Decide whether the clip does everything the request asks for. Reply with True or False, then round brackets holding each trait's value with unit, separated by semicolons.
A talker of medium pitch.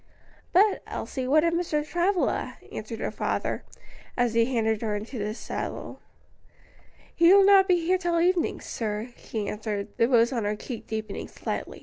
False (255 Hz)